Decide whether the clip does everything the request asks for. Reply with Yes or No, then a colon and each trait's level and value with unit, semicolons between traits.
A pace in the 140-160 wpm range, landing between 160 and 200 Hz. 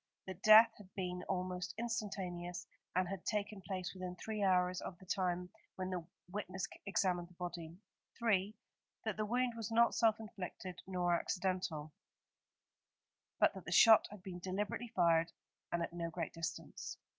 Yes: average, 155 wpm; medium, 185 Hz